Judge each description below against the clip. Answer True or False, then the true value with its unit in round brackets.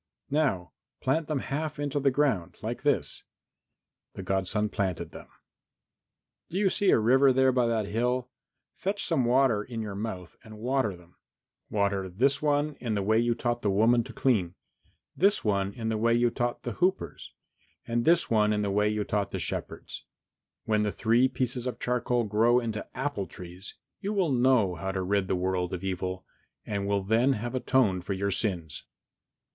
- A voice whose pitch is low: True (115 Hz)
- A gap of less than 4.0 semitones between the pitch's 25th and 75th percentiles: False (4.7 semitones)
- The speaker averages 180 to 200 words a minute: True (185 wpm)